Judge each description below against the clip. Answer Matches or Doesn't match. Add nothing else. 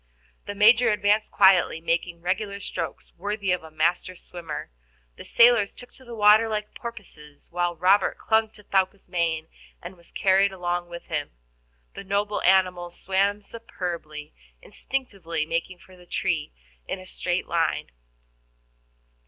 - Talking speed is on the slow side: Doesn't match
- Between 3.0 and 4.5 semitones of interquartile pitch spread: Matches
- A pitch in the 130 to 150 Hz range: Doesn't match